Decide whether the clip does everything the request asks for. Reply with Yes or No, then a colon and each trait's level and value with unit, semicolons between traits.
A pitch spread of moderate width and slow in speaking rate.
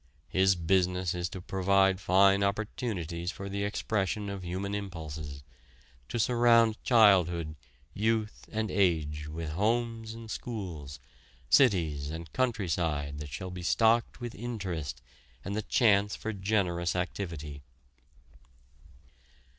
Yes: average, 4.5 semitones; slow, 115 wpm